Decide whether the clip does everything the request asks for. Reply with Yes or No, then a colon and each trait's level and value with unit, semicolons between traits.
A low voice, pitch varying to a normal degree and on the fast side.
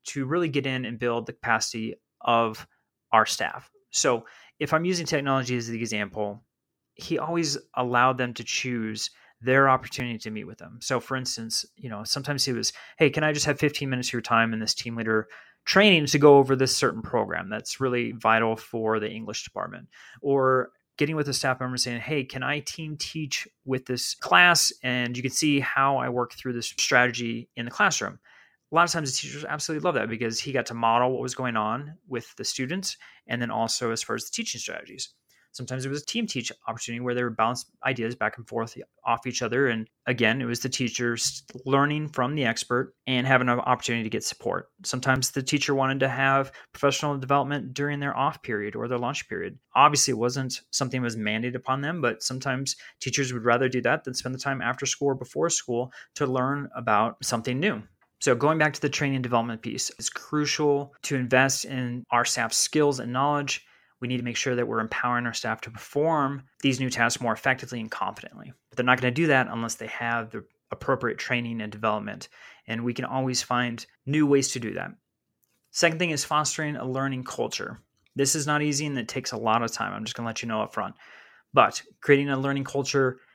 Yes: low, 130 Hz; average, 3.1 semitones; fast, 215 wpm